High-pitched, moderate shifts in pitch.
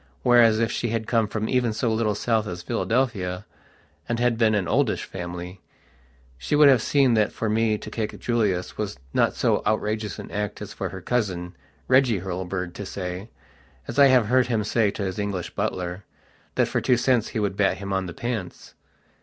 No: low, 110 Hz; average, 3.7 semitones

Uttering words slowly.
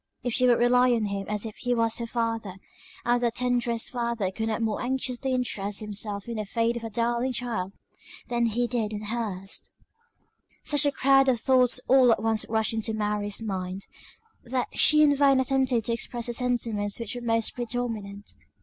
No: average, 195 wpm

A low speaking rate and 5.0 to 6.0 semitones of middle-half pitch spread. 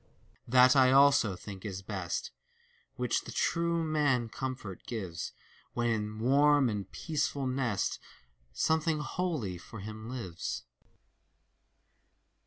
Yes: slow, 110 wpm; wide, 5.6 semitones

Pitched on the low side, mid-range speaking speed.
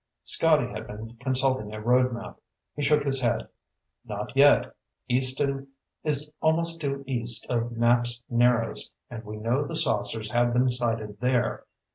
Yes: low, 120 Hz; average, 150 wpm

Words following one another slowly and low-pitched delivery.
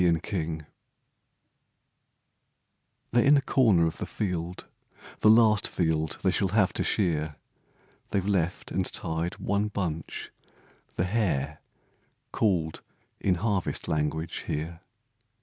Yes: slow, 120 wpm; very low, 90 Hz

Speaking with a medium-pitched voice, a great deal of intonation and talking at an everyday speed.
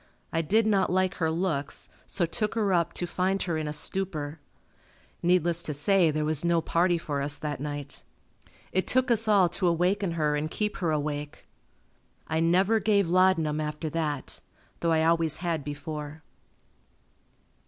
No: medium, 165 Hz; average, 3.6 semitones; average, 165 wpm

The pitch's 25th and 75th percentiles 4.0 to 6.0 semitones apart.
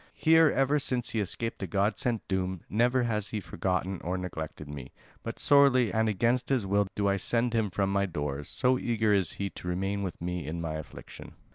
Yes: average, 4.5 semitones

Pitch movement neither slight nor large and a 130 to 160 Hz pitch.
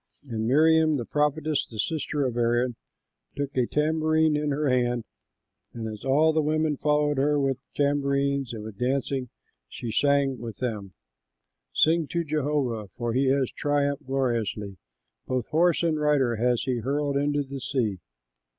Yes: average, 3.5 semitones; medium, 140 Hz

